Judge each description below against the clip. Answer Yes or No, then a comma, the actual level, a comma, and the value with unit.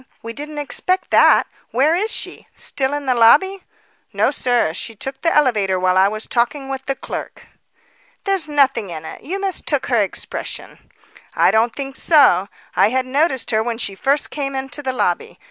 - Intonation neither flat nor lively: Yes, average, 4.4 semitones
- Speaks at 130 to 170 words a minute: No, average, 180 wpm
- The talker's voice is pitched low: No, very high, 265 Hz